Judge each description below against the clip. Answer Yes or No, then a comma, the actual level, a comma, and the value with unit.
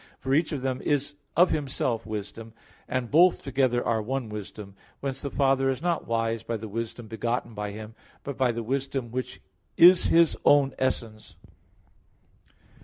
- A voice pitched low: Yes, low, 125 Hz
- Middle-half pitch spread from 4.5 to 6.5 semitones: No, average, 3.4 semitones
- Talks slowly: No, average, 165 wpm